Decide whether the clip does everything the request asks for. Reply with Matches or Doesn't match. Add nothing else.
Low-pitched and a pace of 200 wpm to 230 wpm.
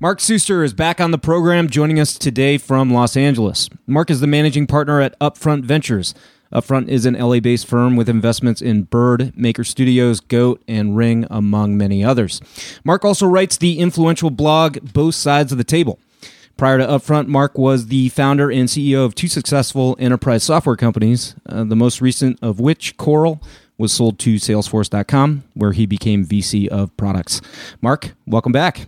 Doesn't match